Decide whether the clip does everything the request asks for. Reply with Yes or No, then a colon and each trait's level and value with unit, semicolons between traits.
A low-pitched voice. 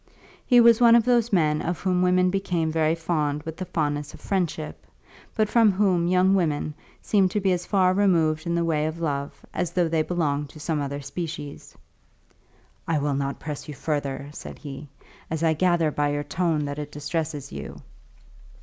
No: medium, 160 Hz